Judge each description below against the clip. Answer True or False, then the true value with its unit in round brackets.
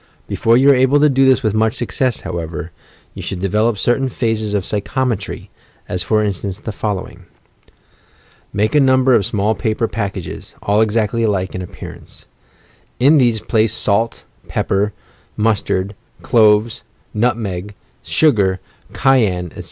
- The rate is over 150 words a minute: False (145 wpm)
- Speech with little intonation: False (3.3 semitones)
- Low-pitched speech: True (110 Hz)